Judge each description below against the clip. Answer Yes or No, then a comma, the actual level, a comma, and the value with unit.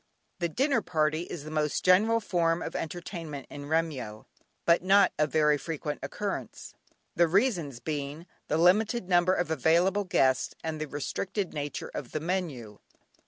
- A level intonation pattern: No, average, 3.6 semitones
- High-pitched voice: No, medium, 165 Hz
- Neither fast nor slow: Yes, average, 155 wpm